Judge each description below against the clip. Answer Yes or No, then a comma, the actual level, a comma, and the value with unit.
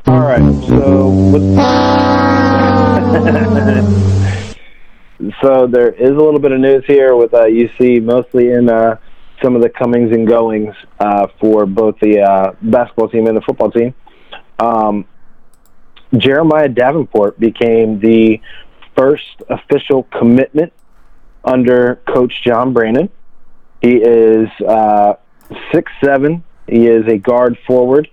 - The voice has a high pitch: No, low, 115 Hz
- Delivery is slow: Yes, slow, 125 wpm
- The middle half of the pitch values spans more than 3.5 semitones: No, average, 2.8 semitones